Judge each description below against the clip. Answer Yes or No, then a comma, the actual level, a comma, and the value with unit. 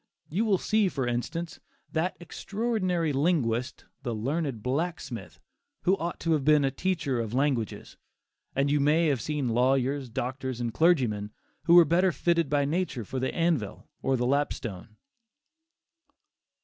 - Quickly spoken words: No, average, 150 wpm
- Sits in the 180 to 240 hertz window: No, medium, 140 Hz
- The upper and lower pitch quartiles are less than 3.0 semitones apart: No, wide, 5.5 semitones